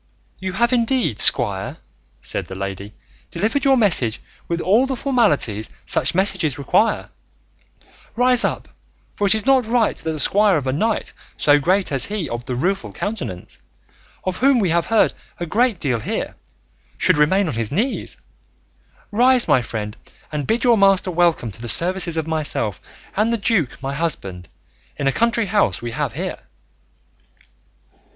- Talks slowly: No, average, 165 wpm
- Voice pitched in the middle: Yes, medium, 180 Hz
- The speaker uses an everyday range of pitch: No, wide, 8.9 semitones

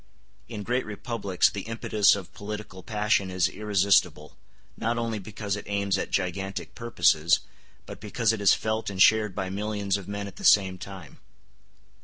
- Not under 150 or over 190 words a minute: Yes, average, 165 wpm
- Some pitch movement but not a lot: No, narrow, 2.0 semitones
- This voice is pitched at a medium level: No, low, 100 Hz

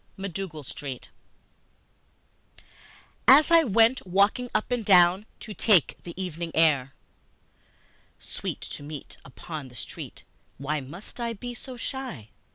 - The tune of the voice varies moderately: No, wide, 7.4 semitones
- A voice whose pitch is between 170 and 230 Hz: Yes, medium, 185 Hz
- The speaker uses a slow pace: Yes, slow, 125 wpm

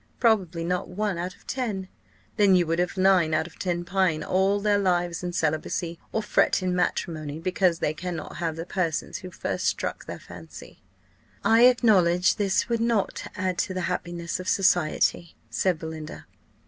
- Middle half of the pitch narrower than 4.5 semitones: Yes, narrow, 2.4 semitones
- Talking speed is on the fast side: No, average, 175 wpm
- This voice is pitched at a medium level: Yes, medium, 180 Hz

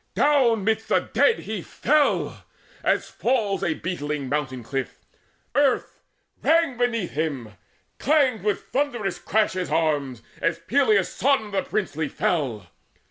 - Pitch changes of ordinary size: No, wide, 8.6 semitones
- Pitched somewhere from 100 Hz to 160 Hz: No, high, 200 Hz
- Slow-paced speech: Yes, slow, 130 wpm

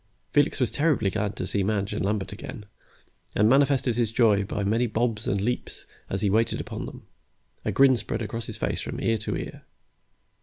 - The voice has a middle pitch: No, low, 110 Hz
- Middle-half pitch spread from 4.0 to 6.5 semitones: No, average, 3.0 semitones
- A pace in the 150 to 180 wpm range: No, average, 195 wpm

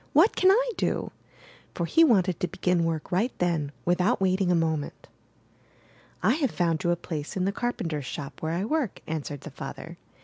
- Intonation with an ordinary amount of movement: No, wide, 5.9 semitones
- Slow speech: No, fast, 205 wpm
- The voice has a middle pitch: Yes, medium, 180 Hz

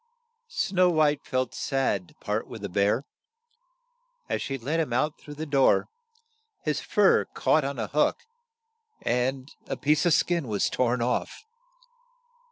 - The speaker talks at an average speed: Yes, average, 155 wpm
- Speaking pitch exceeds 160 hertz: No, medium, 140 Hz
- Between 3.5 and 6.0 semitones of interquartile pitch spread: Yes, average, 3.9 semitones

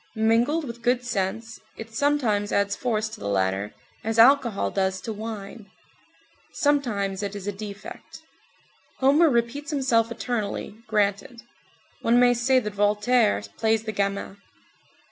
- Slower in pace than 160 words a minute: Yes, slow, 135 wpm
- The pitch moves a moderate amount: Yes, average, 3.3 semitones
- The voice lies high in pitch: Yes, high, 225 Hz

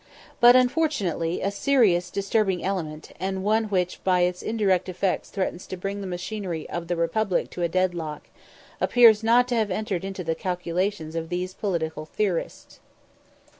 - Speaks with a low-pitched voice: No, medium, 185 Hz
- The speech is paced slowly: No, average, 165 wpm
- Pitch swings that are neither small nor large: Yes, average, 3.3 semitones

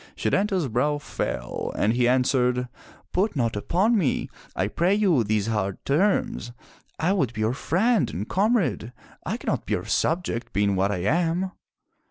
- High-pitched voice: No, low, 135 Hz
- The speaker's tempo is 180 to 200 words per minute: No, average, 170 wpm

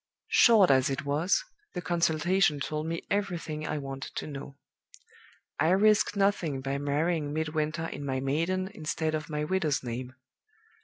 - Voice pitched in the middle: Yes, medium, 155 Hz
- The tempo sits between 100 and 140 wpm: No, average, 150 wpm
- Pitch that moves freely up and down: No, average, 3.6 semitones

